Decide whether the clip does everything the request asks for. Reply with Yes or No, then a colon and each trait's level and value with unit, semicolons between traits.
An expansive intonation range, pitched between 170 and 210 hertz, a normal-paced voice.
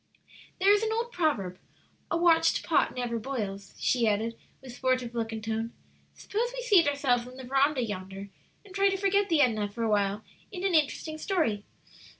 No: wide, 8.0 semitones; very high, 255 Hz; average, 180 wpm